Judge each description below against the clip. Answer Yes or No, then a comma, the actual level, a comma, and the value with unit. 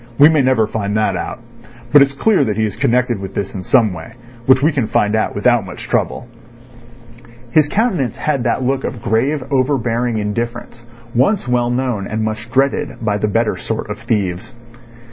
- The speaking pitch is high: No, low, 120 Hz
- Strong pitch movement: No, average, 3.7 semitones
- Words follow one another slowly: No, average, 185 wpm